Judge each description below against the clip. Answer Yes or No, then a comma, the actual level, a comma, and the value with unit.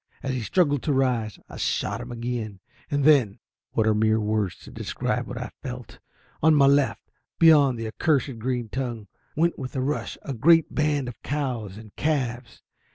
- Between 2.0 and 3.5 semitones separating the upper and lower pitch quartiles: No, average, 4.4 semitones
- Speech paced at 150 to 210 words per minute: Yes, average, 180 wpm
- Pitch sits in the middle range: No, low, 125 Hz